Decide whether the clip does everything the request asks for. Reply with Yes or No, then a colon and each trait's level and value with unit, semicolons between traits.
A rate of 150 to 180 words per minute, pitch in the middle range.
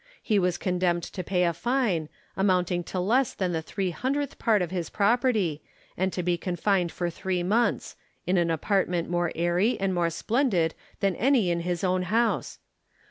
No: average, 190 wpm; medium, 180 Hz